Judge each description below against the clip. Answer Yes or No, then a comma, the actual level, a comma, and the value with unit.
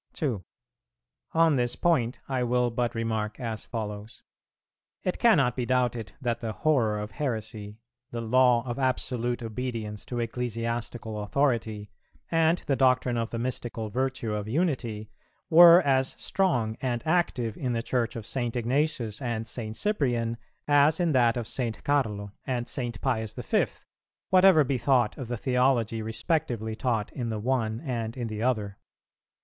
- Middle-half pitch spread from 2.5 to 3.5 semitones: Yes, average, 3.0 semitones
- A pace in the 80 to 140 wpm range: No, average, 155 wpm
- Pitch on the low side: Yes, low, 120 Hz